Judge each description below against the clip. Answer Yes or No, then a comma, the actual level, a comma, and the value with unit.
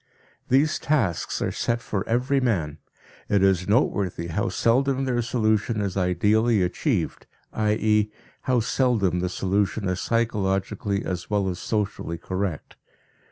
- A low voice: Yes, low, 105 Hz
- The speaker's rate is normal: No, slow, 130 wpm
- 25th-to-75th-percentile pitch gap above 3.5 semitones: Yes, average, 4.1 semitones